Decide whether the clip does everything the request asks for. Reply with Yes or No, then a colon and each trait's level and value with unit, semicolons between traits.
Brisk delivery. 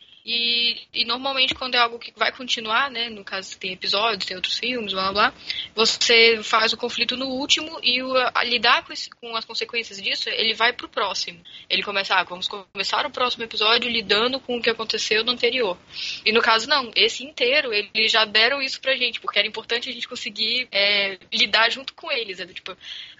Yes: fast, 210 wpm